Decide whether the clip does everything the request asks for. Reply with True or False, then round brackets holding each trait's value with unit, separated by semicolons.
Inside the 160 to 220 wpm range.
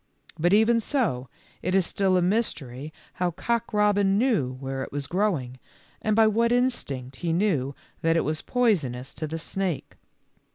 True (165 wpm)